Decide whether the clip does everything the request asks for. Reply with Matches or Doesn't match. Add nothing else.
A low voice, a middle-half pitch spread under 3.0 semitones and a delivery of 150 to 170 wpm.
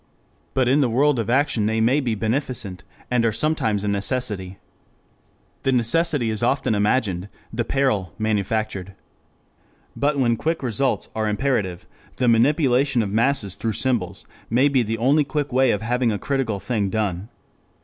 Doesn't match